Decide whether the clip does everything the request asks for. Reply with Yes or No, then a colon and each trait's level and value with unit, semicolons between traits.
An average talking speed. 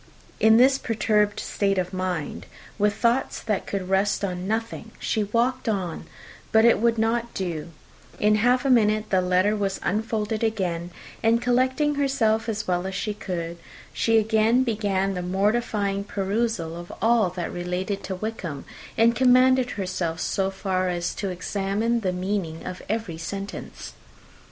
Yes: average, 155 wpm